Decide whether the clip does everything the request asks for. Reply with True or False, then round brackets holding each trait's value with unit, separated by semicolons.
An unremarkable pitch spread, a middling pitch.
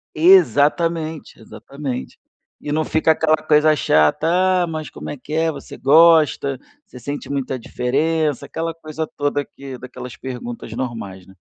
True (3.8 semitones; 150 Hz)